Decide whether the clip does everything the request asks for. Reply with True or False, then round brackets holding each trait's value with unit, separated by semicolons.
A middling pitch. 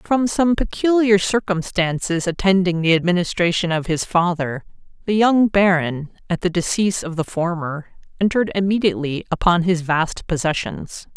True (180 Hz)